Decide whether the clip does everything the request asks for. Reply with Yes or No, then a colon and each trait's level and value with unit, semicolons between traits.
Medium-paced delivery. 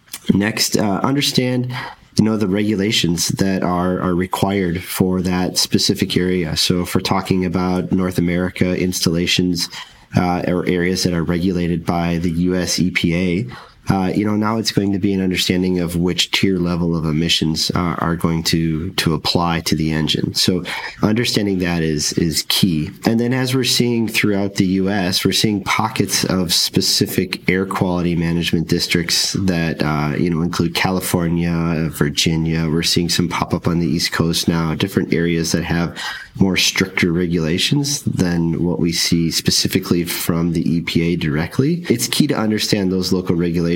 Yes: average, 165 wpm